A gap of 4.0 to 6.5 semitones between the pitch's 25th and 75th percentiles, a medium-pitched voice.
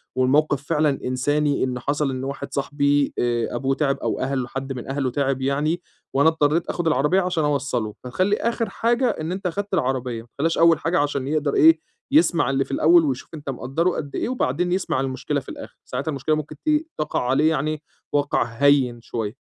No: average, 3.2 semitones; medium, 145 Hz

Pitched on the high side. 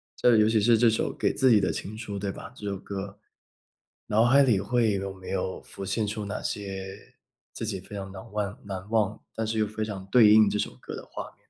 No: low, 105 Hz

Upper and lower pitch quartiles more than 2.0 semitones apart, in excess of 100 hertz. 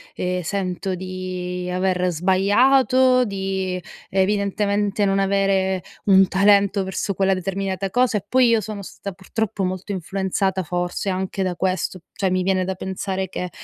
No: narrow, 1.4 semitones; high, 190 Hz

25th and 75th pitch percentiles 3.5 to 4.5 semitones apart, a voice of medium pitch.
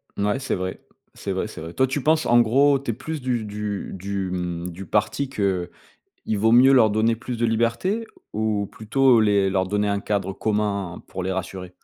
No: average, 3.9 semitones; low, 105 Hz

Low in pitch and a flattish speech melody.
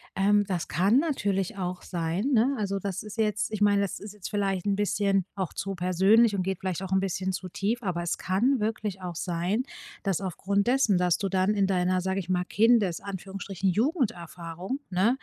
No: high, 195 Hz; narrow, 2.3 semitones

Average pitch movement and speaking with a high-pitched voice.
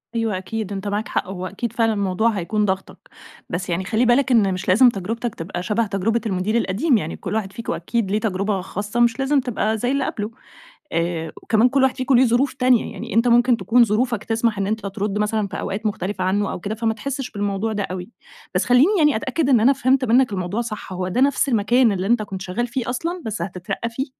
Yes: average, 3.8 semitones; high, 220 Hz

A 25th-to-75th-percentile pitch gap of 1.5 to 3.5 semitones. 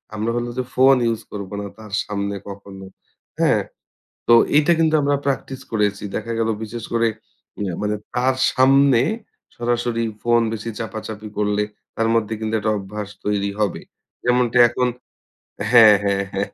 Yes: average, 2.7 semitones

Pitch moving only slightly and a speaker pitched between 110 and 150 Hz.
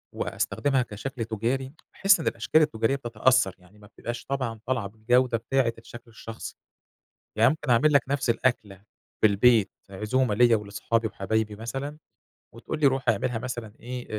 No: average, 3.1 semitones; low, 120 Hz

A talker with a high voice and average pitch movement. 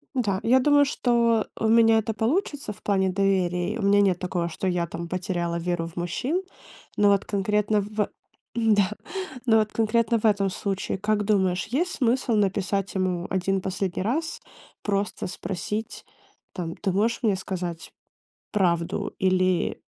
Yes: high, 200 Hz; average, 3.3 semitones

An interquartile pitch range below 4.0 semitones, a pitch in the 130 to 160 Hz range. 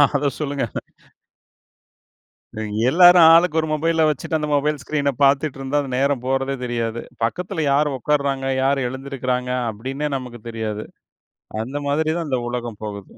Yes: average, 3.2 semitones; medium, 140 Hz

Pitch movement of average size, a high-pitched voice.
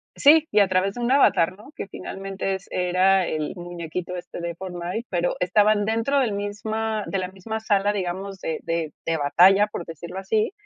Yes: average, 3.2 semitones; high, 195 Hz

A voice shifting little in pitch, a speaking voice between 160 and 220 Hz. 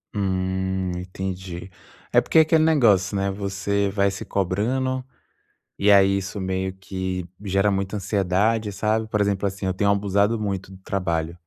No: narrow, 1.5 semitones; low, 100 Hz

